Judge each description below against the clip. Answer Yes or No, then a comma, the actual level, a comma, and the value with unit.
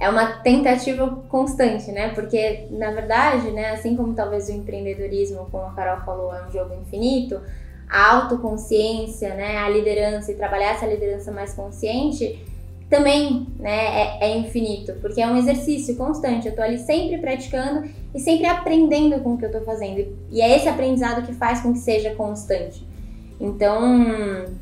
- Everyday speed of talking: Yes, average, 165 wpm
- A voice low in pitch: No, high, 220 Hz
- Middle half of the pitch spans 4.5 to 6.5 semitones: No, average, 3.7 semitones